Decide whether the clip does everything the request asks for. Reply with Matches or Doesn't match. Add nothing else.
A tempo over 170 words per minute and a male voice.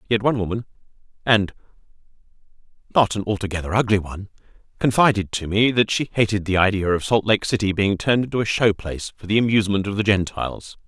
Matches